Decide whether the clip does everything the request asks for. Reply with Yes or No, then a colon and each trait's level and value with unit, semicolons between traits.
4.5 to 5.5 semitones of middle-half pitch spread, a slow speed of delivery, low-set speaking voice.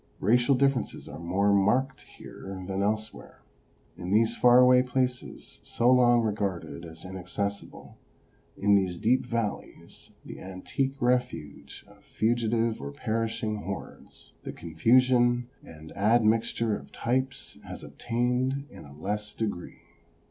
No: average, 4.1 semitones; slow, 125 wpm; low, 110 Hz